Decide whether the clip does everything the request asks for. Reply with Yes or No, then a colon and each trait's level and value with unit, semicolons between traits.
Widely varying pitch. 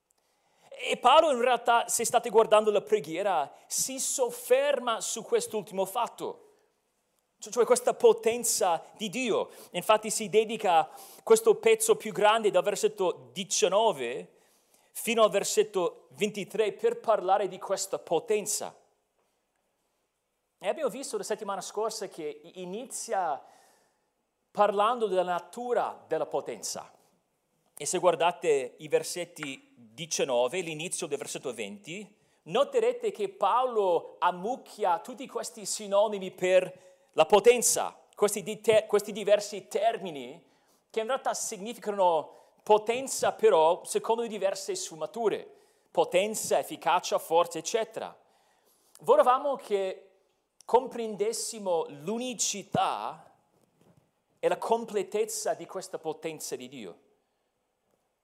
Yes: wide, 8.5 semitones